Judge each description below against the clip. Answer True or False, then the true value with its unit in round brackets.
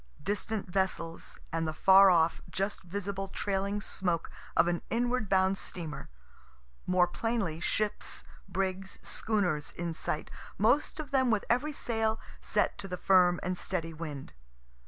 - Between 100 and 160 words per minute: True (140 wpm)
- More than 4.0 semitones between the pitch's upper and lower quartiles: False (3.4 semitones)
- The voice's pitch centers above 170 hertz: True (190 Hz)